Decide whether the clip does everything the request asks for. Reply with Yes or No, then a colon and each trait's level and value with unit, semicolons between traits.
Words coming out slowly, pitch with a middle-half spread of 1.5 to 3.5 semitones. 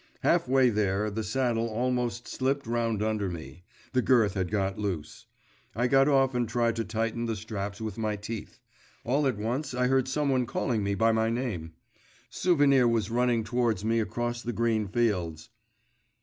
No: average, 175 wpm; average, 2.9 semitones